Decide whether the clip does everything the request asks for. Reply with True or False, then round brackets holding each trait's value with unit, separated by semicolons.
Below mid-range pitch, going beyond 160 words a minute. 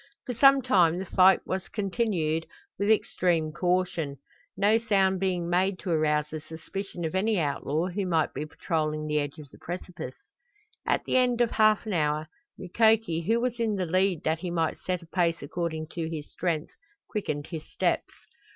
False (175 Hz; 180 wpm)